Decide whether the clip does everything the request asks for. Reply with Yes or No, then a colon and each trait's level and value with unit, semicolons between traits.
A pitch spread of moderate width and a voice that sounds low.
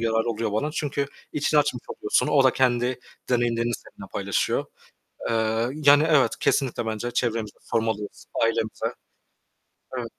Yes: average, 3.8 semitones; low, 120 Hz